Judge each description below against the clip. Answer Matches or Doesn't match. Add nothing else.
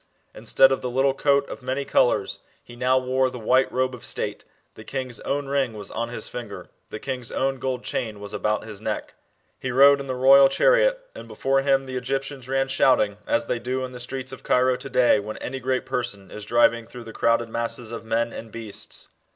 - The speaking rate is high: Matches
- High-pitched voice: Doesn't match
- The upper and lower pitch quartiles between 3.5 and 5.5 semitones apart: Doesn't match